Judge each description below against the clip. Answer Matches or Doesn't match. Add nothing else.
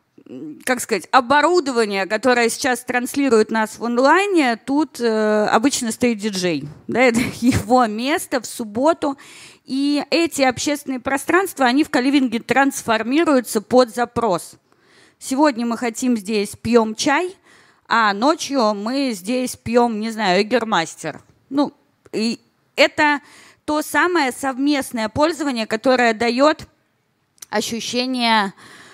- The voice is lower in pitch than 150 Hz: Doesn't match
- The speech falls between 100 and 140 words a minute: Matches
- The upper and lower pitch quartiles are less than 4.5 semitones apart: Matches